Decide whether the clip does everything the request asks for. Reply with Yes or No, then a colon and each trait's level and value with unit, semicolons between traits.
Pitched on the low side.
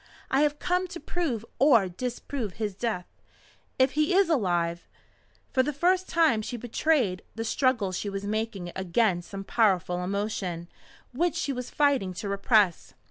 No: high, 225 Hz